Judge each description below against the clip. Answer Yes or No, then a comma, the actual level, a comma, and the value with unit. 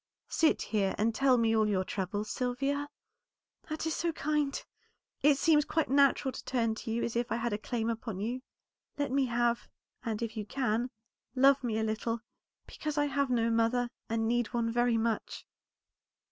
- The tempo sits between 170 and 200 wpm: Yes, average, 185 wpm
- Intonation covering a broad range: No, average, 3.5 semitones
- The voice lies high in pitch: Yes, high, 240 Hz